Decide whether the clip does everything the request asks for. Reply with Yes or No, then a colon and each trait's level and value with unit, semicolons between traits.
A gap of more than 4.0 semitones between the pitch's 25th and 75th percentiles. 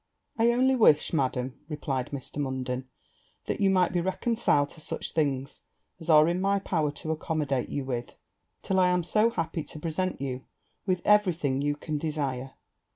Yes: average, 5.1 semitones